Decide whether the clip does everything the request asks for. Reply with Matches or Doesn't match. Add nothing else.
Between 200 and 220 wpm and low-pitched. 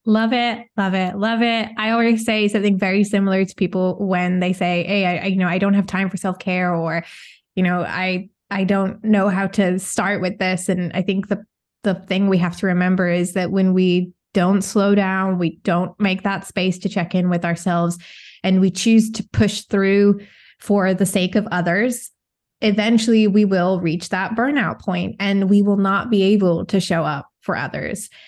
Doesn't match